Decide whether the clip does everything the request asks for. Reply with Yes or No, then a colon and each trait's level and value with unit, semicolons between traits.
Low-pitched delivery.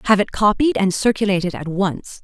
No: high, 200 Hz